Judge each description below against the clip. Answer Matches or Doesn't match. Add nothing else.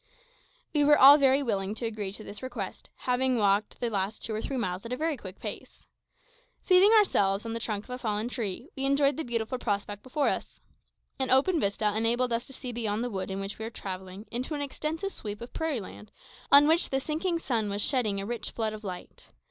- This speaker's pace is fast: Matches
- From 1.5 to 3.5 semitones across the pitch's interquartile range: Doesn't match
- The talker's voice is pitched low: Doesn't match